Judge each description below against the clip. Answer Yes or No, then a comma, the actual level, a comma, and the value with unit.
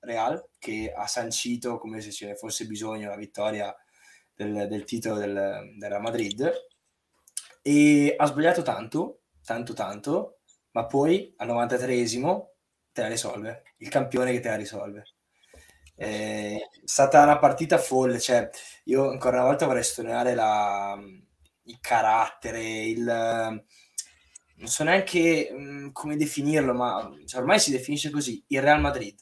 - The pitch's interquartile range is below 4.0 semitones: No, average, 5.3 semitones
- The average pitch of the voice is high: No, low, 120 Hz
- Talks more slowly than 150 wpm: Yes, average, 140 wpm